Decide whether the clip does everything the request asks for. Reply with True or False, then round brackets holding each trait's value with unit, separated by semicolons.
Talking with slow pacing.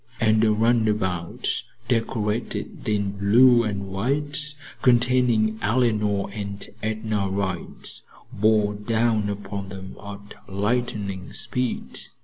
True (100 wpm)